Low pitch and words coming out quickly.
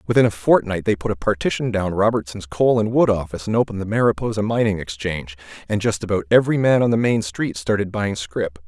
Yes: low, 100 Hz; fast, 215 wpm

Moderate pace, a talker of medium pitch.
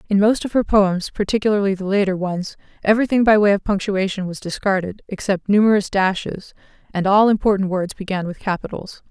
No: average, 170 wpm; high, 200 Hz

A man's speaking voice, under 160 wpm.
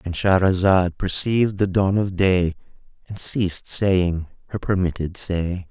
Yes: male; slow, 135 wpm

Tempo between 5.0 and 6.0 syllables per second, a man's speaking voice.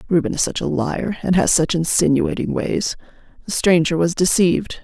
No: 5.1 syllables/s; female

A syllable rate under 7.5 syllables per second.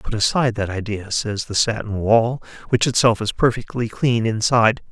Yes: 5.1 syllables/s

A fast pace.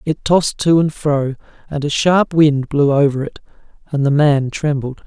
No: average, 190 wpm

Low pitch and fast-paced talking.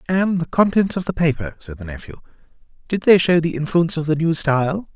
No: medium, 160 Hz; fast, 220 wpm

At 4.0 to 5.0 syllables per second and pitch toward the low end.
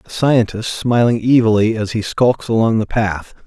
Yes: 4.5 syllables/s; low, 110 Hz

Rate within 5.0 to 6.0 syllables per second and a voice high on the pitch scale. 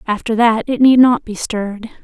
Yes: 5.1 syllables/s; high, 230 Hz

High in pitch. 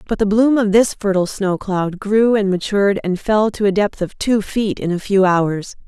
Yes: high, 200 Hz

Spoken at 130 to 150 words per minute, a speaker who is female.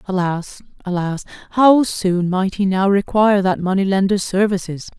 Yes: average, 145 wpm; female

